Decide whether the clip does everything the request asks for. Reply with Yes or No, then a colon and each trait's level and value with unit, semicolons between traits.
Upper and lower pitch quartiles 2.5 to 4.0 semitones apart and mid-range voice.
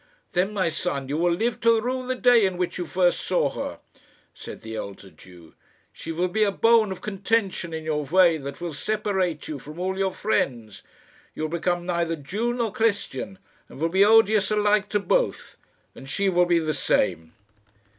No: average, 5.1 semitones; medium, 180 Hz